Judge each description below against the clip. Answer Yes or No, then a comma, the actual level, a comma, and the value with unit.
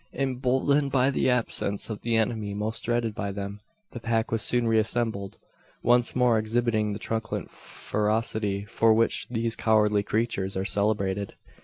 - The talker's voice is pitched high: No, low, 110 Hz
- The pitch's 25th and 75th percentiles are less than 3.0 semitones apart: Yes, narrow, 2.4 semitones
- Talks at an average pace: Yes, average, 150 wpm